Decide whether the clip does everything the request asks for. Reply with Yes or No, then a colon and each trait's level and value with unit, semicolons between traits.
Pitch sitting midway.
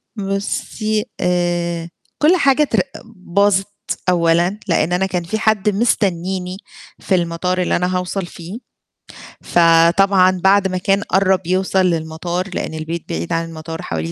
Yes: medium, 180 Hz